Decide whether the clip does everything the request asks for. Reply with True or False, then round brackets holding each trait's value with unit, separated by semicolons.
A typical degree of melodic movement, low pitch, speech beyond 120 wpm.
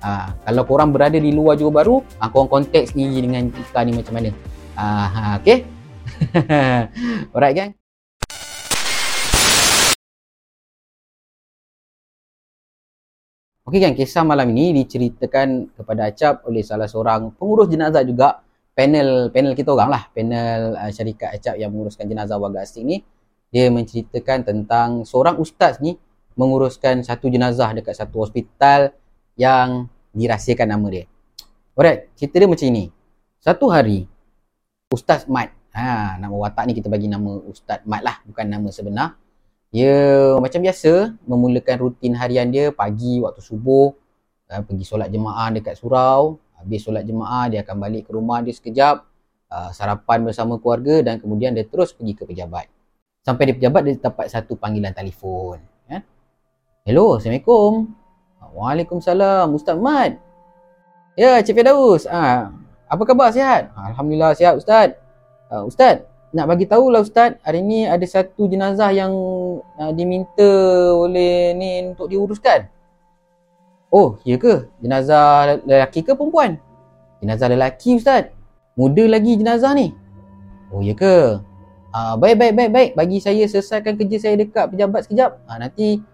False (8.2 semitones; 130 Hz; 140 wpm)